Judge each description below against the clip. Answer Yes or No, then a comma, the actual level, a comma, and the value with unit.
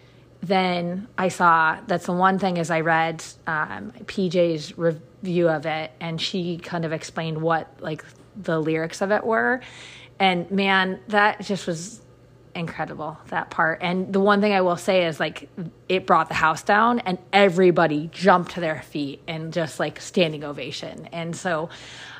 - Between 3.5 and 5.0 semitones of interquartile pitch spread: No, average, 2.9 semitones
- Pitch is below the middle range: No, medium, 170 Hz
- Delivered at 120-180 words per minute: Yes, average, 170 wpm